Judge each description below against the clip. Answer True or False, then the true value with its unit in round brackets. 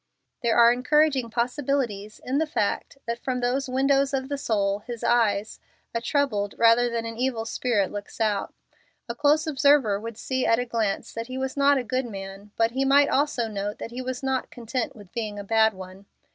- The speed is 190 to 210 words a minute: True (200 wpm)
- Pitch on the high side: True (235 Hz)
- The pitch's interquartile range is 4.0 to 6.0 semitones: False (3.5 semitones)